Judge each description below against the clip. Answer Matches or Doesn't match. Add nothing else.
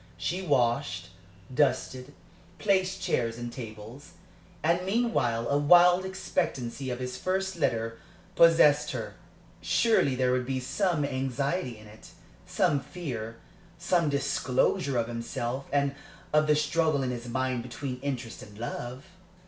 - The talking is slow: Matches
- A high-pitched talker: Doesn't match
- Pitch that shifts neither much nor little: Doesn't match